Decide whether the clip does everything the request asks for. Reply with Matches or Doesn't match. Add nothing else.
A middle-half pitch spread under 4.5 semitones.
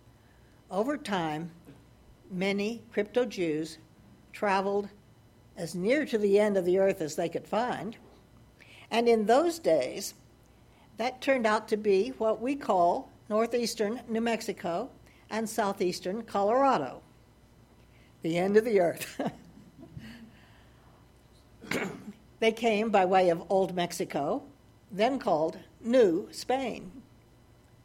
Doesn't match